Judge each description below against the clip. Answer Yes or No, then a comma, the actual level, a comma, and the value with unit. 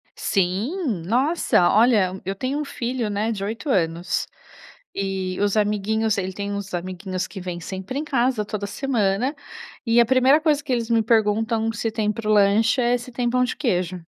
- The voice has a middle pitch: No, high, 215 Hz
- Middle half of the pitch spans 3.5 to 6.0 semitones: Yes, average, 4.1 semitones